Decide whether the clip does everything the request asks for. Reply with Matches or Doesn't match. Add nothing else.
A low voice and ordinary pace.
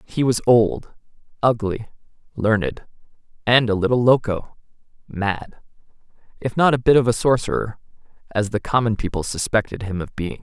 Doesn't match